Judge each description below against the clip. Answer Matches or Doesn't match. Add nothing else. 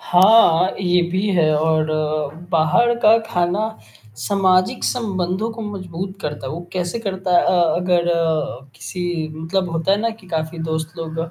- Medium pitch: Matches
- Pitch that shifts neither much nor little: Matches